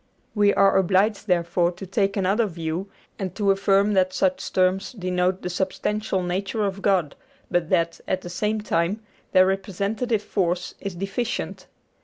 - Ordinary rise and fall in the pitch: No, narrow, 2.0 semitones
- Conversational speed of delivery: Yes, average, 155 wpm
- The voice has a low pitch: No, high, 190 Hz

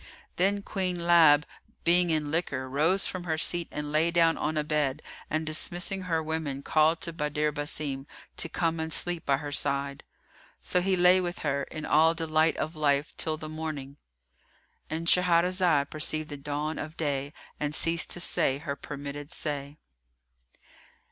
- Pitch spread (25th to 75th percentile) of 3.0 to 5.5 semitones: No, narrow, 2.6 semitones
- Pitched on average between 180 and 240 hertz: No, medium, 155 Hz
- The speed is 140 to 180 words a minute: Yes, average, 160 wpm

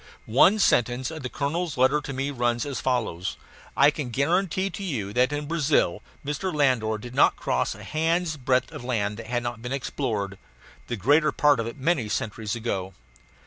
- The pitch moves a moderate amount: Yes, average, 4.3 semitones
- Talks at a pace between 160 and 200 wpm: Yes, average, 185 wpm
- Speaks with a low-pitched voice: Yes, low, 130 Hz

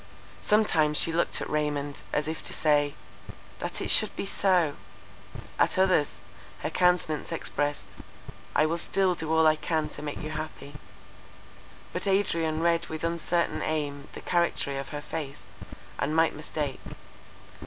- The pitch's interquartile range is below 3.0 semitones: Yes, narrow, 2.4 semitones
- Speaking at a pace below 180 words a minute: Yes, average, 145 wpm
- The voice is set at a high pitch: No, medium, 155 Hz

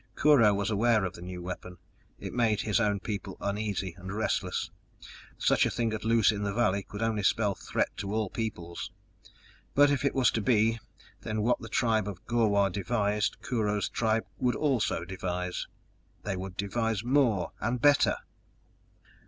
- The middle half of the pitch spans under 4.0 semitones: Yes, average, 2.8 semitones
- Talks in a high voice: No, low, 105 Hz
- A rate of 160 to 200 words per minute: Yes, average, 170 wpm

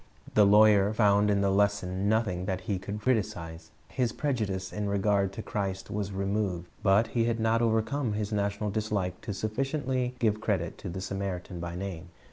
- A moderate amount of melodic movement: No, narrow, 2.2 semitones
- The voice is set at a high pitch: No, low, 100 Hz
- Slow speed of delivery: No, average, 175 wpm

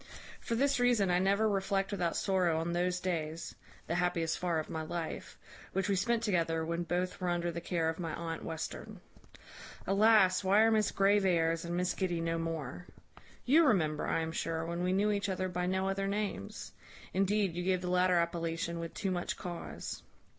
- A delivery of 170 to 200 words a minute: Yes, average, 190 wpm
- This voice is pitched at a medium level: Yes, medium, 180 Hz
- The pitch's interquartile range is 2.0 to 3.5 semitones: Yes, average, 2.8 semitones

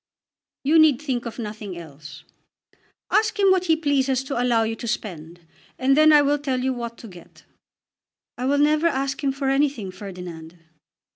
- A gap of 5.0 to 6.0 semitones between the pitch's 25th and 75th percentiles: Yes, wide, 5.6 semitones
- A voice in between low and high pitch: No, very high, 260 Hz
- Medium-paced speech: Yes, average, 180 wpm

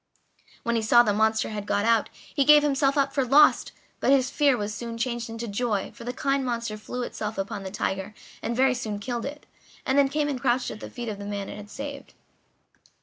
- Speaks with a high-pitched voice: Yes, high, 235 Hz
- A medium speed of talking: No, fast, 230 wpm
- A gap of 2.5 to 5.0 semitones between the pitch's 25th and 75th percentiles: Yes, average, 4.2 semitones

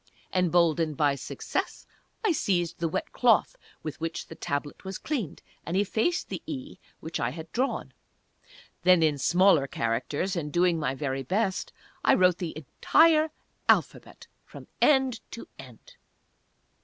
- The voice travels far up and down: Yes, wide, 6.5 semitones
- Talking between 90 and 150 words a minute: Yes, average, 145 wpm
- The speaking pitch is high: No, medium, 175 Hz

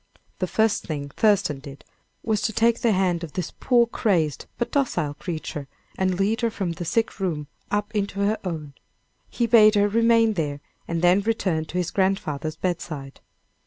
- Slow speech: No, average, 175 wpm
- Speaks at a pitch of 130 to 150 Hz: No, high, 190 Hz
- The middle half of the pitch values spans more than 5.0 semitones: Yes, wide, 5.5 semitones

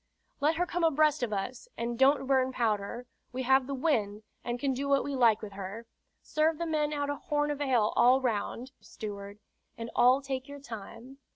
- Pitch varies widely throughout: No, average, 3.8 semitones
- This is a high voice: Yes, very high, 260 Hz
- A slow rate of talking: No, average, 200 wpm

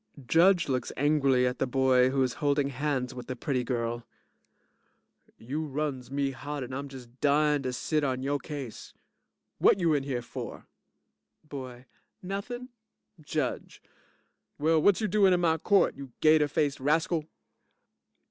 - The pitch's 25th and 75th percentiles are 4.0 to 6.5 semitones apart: No, average, 3.2 semitones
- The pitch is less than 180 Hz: Yes, medium, 140 Hz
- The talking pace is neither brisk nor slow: Yes, average, 150 wpm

